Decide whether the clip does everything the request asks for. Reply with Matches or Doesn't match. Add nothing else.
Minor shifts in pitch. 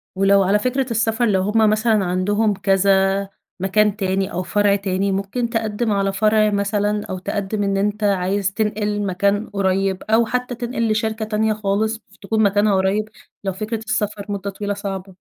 Matches